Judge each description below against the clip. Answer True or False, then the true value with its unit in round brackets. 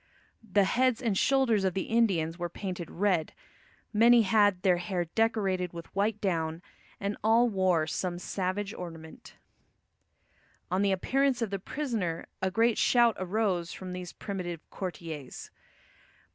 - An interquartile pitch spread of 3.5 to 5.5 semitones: True (4.0 semitones)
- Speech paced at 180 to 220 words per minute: False (140 wpm)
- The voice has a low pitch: False (190 Hz)